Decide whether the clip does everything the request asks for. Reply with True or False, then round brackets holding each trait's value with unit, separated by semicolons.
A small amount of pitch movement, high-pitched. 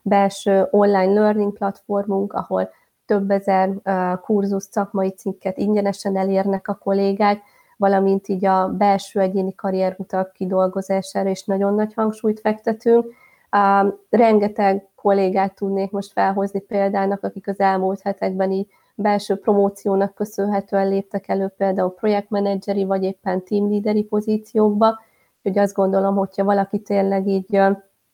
True (0.9 semitones; 195 Hz)